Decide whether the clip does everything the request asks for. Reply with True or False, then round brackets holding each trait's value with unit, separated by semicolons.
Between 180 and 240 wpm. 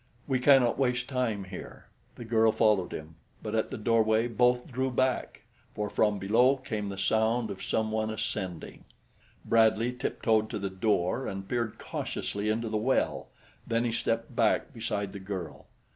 False (165 wpm)